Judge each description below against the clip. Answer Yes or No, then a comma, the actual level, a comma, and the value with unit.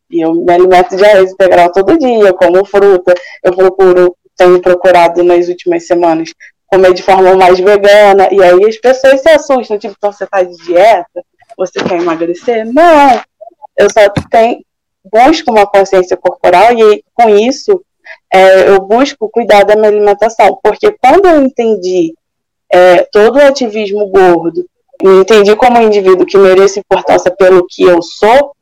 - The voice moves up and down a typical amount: Yes, average, 4.0 semitones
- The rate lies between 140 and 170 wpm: Yes, average, 160 wpm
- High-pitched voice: Yes, high, 195 Hz